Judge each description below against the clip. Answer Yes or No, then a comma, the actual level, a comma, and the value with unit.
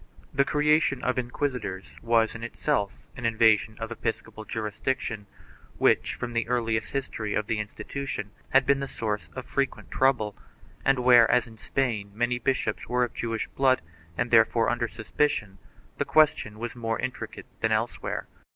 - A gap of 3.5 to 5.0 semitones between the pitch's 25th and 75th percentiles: No, average, 2.8 semitones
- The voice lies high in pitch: No, low, 120 Hz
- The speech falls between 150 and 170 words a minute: Yes, average, 160 wpm